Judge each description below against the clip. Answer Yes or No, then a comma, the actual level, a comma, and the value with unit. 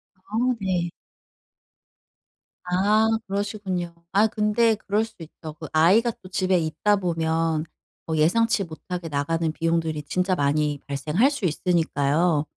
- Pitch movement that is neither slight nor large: Yes, average, 4.3 semitones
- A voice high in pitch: No, medium, 175 Hz